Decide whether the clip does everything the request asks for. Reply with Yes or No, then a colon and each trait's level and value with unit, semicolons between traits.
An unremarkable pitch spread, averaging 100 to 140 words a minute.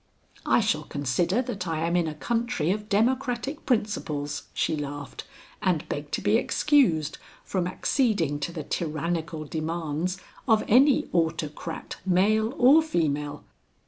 No: wide, 6.5 semitones; slow, 135 wpm